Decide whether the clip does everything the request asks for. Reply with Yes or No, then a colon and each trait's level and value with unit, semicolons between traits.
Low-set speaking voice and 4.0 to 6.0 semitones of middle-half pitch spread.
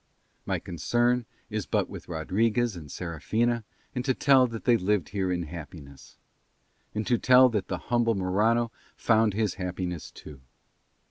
Yes: low, 105 Hz; average, 5.0 semitones